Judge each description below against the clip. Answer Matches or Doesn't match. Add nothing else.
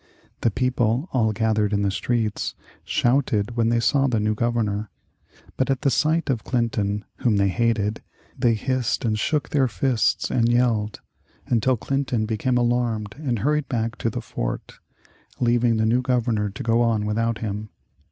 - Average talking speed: Matches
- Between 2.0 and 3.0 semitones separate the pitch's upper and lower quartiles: Matches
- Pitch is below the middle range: Matches